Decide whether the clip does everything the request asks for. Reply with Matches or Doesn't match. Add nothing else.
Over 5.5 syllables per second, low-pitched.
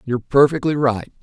Matches